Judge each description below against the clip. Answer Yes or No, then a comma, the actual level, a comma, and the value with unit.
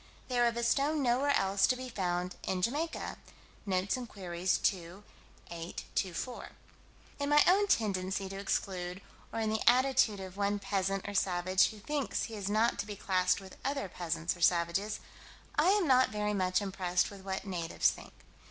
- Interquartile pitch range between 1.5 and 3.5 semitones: No, average, 4.5 semitones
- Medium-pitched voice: No, high, 200 Hz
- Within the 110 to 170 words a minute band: No, average, 180 wpm